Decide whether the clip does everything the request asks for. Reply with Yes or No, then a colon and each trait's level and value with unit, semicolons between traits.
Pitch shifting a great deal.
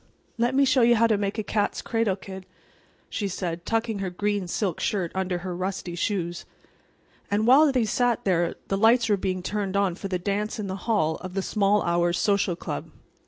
No: average, 3.1 semitones